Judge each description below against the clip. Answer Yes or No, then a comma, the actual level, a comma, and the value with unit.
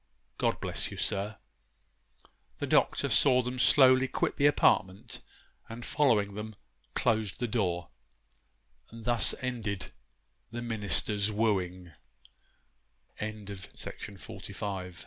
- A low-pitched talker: Yes, low, 110 Hz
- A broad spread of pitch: No, average, 3.6 semitones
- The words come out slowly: Yes, slow, 95 wpm